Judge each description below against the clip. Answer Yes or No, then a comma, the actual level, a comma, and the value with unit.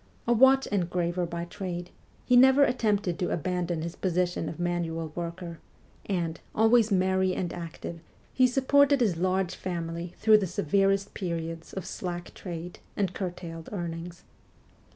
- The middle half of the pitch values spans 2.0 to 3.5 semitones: Yes, average, 2.9 semitones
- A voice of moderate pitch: Yes, medium, 180 Hz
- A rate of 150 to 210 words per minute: No, average, 140 wpm